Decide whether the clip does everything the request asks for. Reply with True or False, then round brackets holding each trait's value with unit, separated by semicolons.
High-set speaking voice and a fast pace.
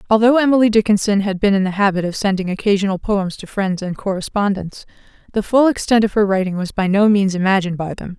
True (200 Hz; 215 wpm)